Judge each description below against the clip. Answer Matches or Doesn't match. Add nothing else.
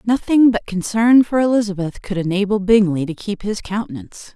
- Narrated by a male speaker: Doesn't match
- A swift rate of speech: Doesn't match